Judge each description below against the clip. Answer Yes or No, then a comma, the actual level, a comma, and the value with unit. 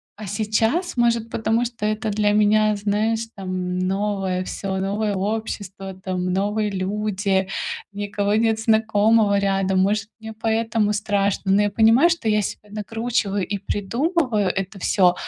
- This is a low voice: No, high, 210 Hz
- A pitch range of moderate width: No, narrow, 2.2 semitones